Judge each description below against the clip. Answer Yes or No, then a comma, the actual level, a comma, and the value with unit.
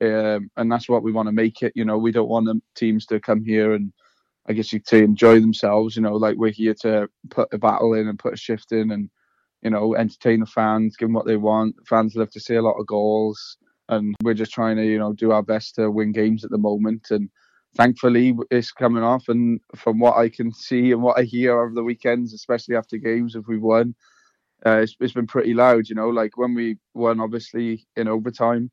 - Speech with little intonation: Yes, narrow, 1.4 semitones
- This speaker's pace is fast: Yes, fast, 240 wpm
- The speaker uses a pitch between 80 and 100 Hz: No, low, 110 Hz